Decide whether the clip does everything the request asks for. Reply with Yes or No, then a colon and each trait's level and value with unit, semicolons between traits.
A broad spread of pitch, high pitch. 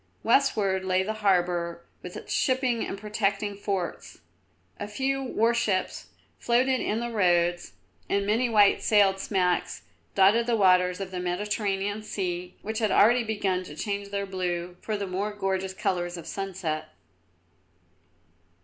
No: average, 2.9 semitones; high, 200 Hz